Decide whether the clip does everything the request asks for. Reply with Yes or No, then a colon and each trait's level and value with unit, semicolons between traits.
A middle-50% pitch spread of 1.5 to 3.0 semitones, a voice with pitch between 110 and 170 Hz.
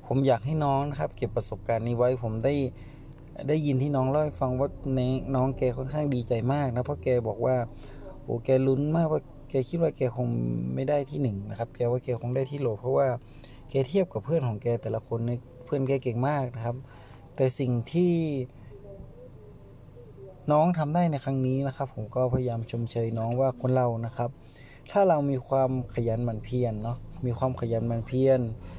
Yes: narrow, 2.6 semitones; low, 130 Hz